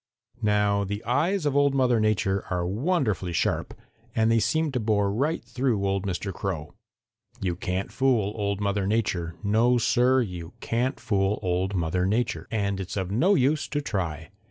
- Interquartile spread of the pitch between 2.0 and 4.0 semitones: No, average, 4.5 semitones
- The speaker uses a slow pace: No, average, 170 wpm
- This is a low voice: Yes, low, 105 Hz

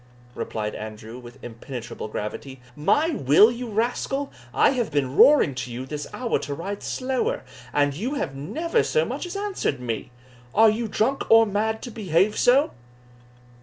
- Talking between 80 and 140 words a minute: No, average, 165 wpm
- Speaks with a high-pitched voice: Yes, high, 205 Hz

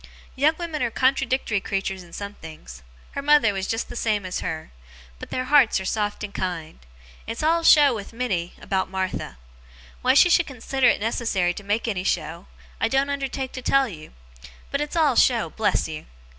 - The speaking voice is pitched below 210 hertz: No, high, 225 Hz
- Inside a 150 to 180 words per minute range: No, average, 190 wpm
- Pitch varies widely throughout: Yes, wide, 6.2 semitones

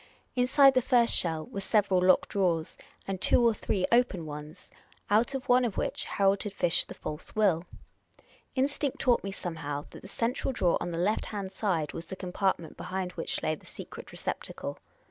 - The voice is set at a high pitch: Yes, high, 195 Hz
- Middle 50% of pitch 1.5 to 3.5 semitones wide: No, wide, 5.6 semitones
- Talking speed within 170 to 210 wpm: Yes, average, 185 wpm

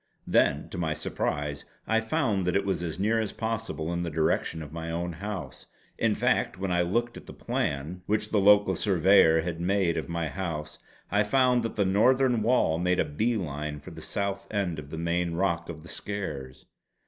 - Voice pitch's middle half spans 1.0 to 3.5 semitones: No, average, 4.3 semitones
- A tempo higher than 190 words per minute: Yes, fast, 205 wpm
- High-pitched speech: No, very low, 90 Hz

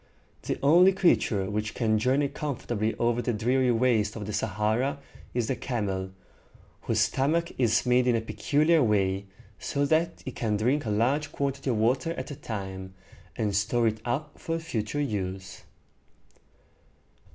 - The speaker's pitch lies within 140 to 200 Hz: No, low, 120 Hz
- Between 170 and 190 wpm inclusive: No, average, 160 wpm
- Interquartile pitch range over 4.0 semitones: Yes, average, 4.7 semitones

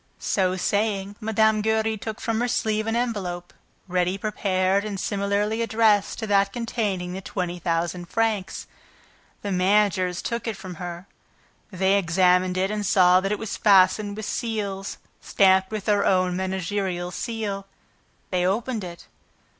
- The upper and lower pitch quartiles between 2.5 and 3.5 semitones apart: Yes, average, 2.8 semitones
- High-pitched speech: Yes, high, 200 Hz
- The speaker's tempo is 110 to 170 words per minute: Yes, average, 145 wpm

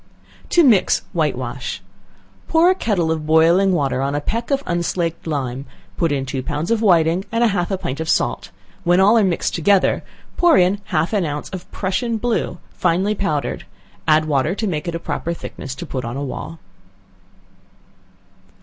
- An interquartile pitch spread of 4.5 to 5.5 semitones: Yes, average, 4.9 semitones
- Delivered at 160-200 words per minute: Yes, average, 180 wpm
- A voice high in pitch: No, medium, 170 Hz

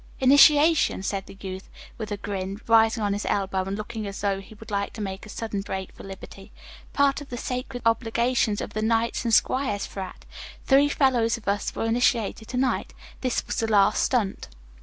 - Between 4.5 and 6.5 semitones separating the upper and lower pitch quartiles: No, average, 3.6 semitones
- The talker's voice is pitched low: No, high, 220 Hz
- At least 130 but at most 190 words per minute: No, average, 200 wpm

